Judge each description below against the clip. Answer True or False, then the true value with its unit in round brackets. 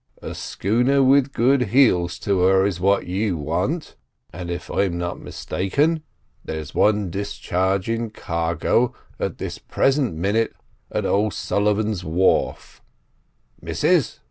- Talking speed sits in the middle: False (115 wpm)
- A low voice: True (100 Hz)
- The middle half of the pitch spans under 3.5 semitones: False (4.5 semitones)